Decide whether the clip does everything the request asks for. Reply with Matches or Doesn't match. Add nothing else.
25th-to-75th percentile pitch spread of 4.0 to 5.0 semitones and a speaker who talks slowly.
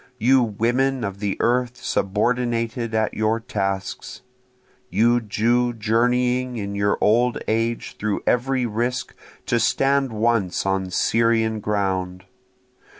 Doesn't match